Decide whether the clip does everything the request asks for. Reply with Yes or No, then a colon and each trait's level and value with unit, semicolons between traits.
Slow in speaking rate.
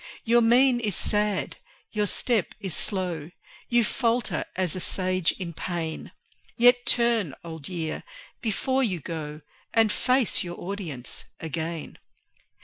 Yes: slow, 130 wpm